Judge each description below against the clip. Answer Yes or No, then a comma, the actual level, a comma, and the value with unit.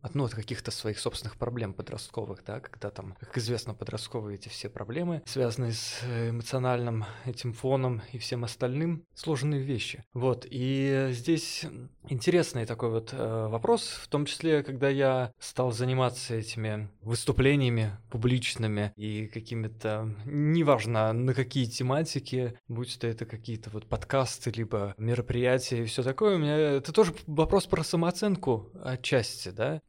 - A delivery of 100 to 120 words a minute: No, average, 145 wpm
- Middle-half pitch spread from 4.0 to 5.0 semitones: No, average, 3.4 semitones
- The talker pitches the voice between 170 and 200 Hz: No, low, 125 Hz